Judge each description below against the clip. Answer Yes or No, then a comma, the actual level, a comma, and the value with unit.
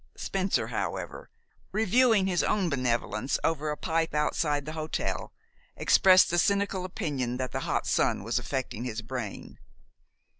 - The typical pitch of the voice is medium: Yes, medium, 155 Hz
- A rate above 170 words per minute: No, average, 140 wpm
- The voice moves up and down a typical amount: No, wide, 6.5 semitones